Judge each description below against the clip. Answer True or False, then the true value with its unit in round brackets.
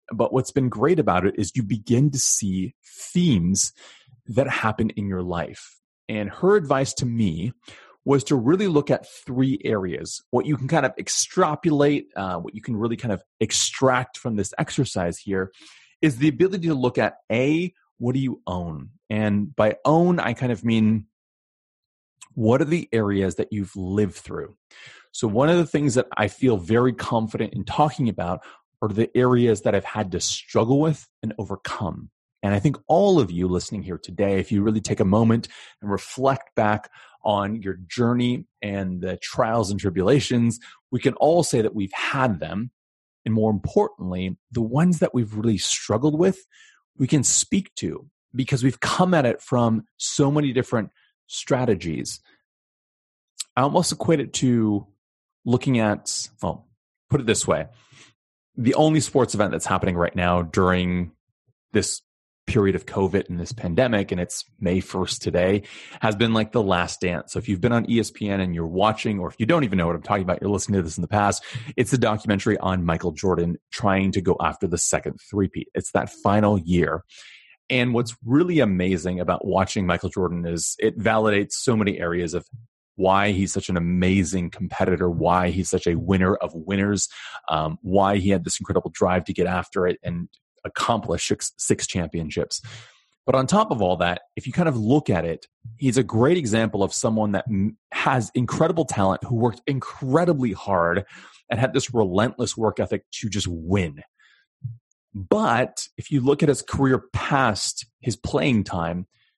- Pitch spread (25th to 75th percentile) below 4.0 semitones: False (5.2 semitones)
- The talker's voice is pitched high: False (110 Hz)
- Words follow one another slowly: False (180 wpm)